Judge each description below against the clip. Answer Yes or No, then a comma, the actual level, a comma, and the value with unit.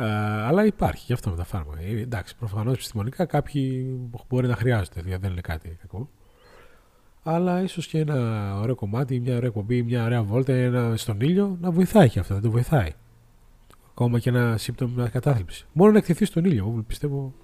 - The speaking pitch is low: Yes, low, 120 Hz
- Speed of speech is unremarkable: No, fast, 180 wpm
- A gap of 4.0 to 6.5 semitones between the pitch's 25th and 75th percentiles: Yes, average, 4.5 semitones